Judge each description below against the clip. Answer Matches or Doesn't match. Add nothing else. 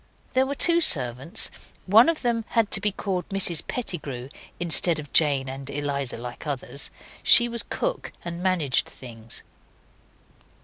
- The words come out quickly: Doesn't match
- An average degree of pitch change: Doesn't match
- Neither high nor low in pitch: Matches